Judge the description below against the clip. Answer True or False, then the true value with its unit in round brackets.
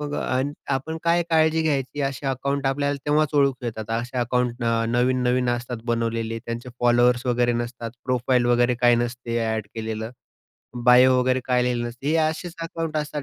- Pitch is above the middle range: False (125 Hz)